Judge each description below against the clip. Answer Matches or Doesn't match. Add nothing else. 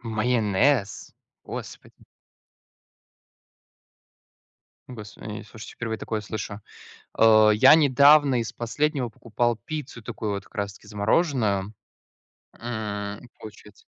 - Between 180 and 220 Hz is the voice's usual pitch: Doesn't match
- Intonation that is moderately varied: Matches